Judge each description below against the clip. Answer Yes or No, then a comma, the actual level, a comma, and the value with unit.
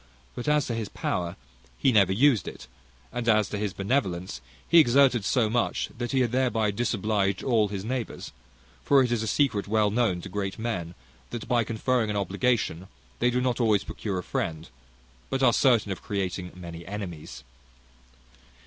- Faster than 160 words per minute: Yes, average, 175 wpm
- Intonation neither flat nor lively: Yes, average, 4.0 semitones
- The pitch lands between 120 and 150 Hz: No, low, 110 Hz